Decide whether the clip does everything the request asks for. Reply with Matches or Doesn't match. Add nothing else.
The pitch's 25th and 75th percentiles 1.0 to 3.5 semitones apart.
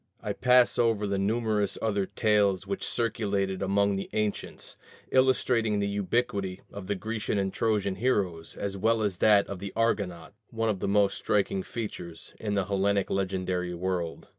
Matches